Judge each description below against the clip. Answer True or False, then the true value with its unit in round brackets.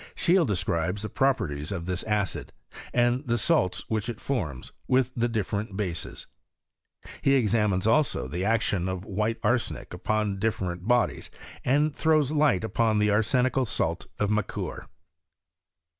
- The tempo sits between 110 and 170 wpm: True (145 wpm)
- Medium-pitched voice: False (110 Hz)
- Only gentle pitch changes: False (4.7 semitones)